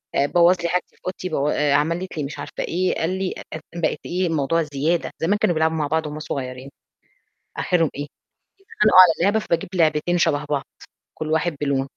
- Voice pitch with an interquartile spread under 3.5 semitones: Yes, average, 3.1 semitones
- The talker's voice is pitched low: No, medium, 160 Hz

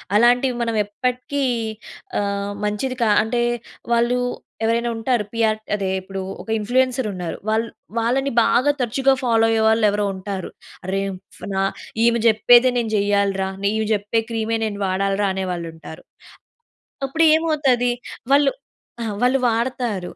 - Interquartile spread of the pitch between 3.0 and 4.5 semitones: Yes, average, 3.4 semitones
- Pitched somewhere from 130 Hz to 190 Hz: No, high, 225 Hz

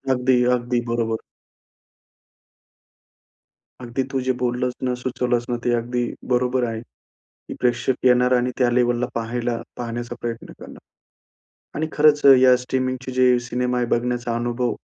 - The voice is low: Yes, low, 125 Hz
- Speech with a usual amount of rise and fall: No, narrow, 0.9 semitones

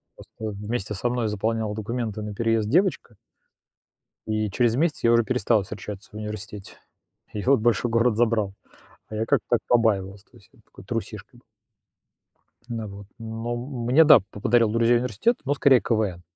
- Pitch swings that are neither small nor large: No, narrow, 2.3 semitones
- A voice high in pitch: No, low, 115 Hz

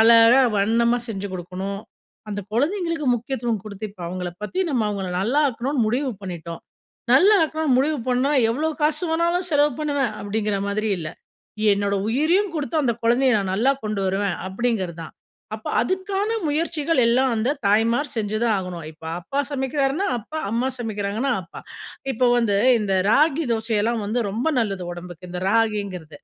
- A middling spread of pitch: No, wide, 6.1 semitones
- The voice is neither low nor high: No, high, 230 Hz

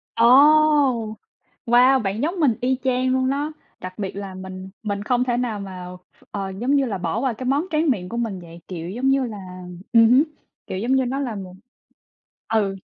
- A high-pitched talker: Yes, high, 230 Hz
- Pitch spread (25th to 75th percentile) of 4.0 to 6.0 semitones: Yes, average, 5.2 semitones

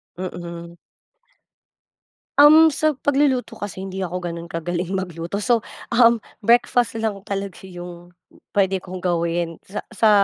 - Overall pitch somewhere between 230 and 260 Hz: No, high, 190 Hz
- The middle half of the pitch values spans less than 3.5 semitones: No, average, 5.0 semitones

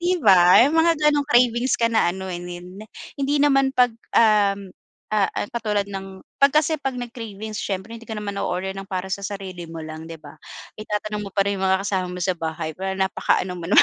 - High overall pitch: Yes, high, 200 Hz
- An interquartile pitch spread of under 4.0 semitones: No, average, 4.3 semitones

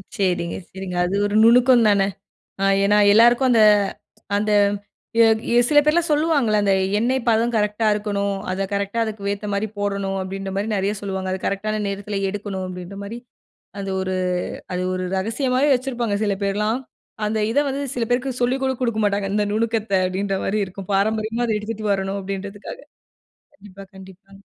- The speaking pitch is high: Yes, high, 205 Hz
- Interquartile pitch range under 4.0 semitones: Yes, average, 2.8 semitones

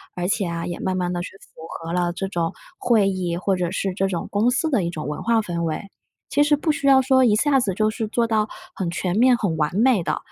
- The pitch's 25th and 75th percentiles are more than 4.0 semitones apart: Yes, average, 5.1 semitones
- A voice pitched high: Yes, high, 195 Hz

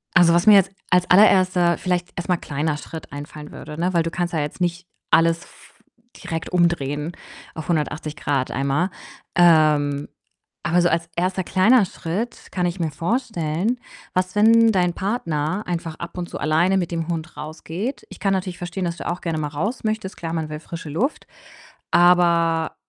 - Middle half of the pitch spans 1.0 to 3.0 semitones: Yes, narrow, 2.5 semitones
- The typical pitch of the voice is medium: Yes, medium, 170 Hz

